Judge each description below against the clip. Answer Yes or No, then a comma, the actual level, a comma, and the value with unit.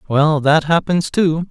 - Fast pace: No, average, 160 wpm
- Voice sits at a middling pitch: Yes, medium, 160 Hz